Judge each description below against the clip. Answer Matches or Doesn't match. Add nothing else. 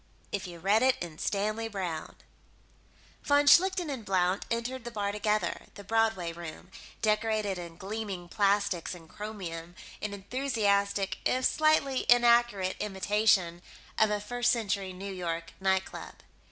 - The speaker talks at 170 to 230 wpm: Doesn't match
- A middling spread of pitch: Matches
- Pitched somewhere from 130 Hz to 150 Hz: Doesn't match